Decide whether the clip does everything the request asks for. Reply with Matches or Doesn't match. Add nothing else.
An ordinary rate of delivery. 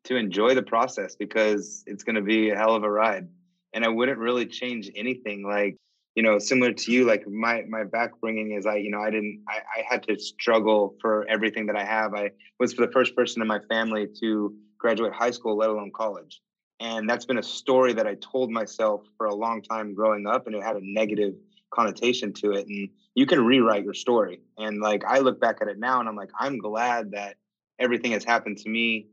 Doesn't match